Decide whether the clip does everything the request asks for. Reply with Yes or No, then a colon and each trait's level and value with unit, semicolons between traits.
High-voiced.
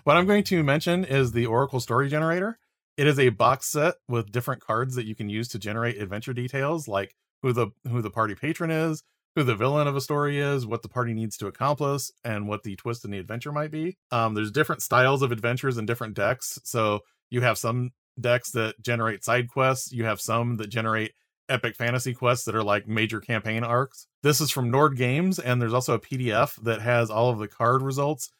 No: low, 125 Hz